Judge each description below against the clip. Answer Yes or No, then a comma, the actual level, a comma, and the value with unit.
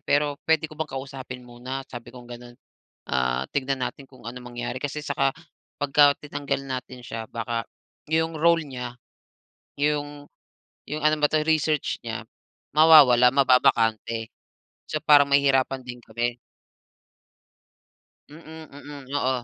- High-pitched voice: No, low, 135 Hz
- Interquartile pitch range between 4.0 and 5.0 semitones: No, average, 3.2 semitones